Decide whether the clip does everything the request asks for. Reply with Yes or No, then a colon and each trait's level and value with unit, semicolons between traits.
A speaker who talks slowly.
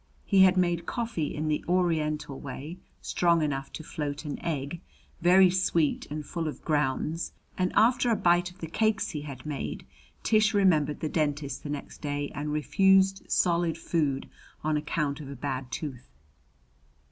No: average, 165 wpm